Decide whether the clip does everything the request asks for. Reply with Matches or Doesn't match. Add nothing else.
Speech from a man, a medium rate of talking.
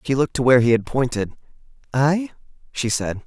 Matches